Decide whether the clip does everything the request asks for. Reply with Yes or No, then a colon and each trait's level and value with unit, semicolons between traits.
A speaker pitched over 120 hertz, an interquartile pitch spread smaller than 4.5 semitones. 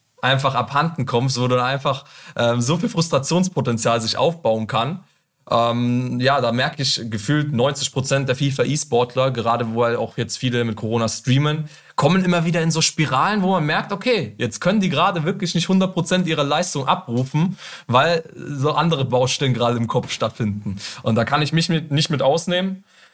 No: medium, 140 Hz; wide, 5.6 semitones